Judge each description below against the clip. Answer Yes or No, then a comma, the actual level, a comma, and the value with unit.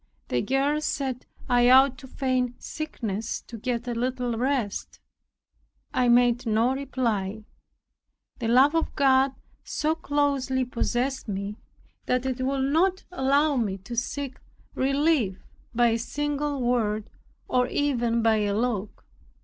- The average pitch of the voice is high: Yes, very high, 250 Hz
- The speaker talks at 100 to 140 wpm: Yes, slow, 135 wpm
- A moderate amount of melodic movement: Yes, average, 3.0 semitones